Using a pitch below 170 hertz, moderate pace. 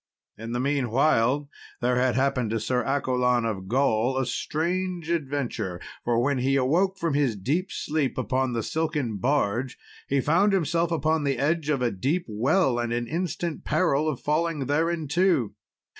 Yes: medium, 140 Hz; average, 160 wpm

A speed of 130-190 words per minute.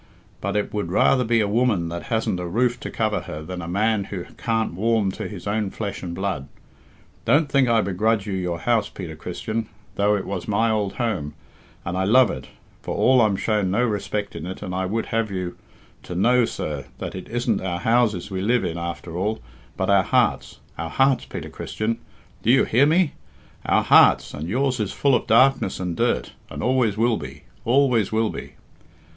No: average, 200 wpm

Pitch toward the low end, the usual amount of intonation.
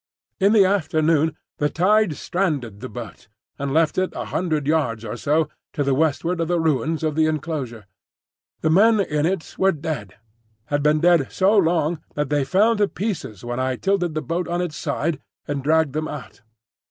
No: medium, 155 Hz; average, 3.7 semitones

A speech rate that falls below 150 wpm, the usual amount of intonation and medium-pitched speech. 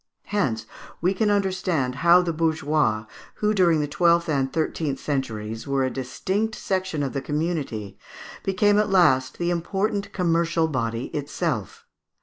No: average, 140 wpm; wide, 5.7 semitones; medium, 165 Hz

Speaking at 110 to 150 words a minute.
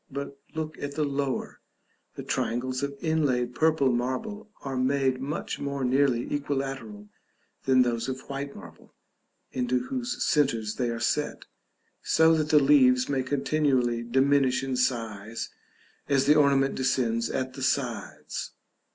Yes: average, 140 wpm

